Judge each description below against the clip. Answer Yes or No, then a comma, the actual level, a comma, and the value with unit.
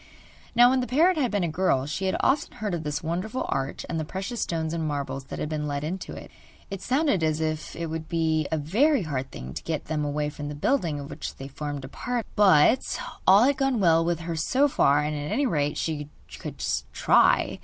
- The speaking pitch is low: No, medium, 160 Hz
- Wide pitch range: Yes, wide, 6.0 semitones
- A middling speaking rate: No, fast, 235 wpm